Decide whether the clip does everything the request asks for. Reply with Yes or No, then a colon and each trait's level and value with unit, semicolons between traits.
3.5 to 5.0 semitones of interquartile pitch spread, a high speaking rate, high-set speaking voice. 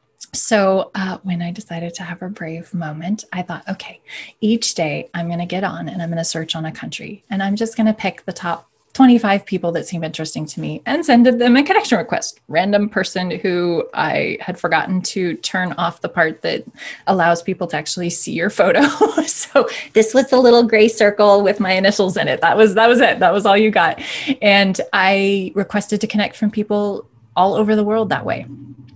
Yes: average, 3.9 semitones; fast, 215 wpm; high, 195 Hz